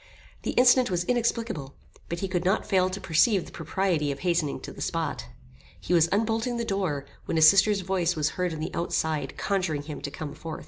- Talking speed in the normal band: No, fast, 210 wpm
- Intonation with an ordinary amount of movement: Yes, average, 4.2 semitones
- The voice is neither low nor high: Yes, medium, 180 Hz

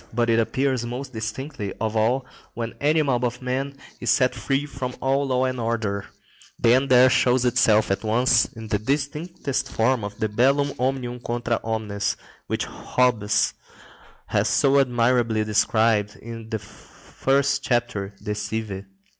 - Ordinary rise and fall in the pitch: Yes, average, 3.1 semitones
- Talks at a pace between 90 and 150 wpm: Yes, average, 145 wpm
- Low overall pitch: Yes, low, 120 Hz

